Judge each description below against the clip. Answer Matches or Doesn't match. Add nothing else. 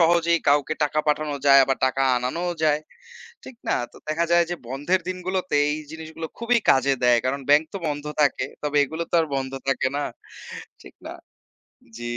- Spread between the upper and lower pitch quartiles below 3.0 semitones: Doesn't match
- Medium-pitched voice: Matches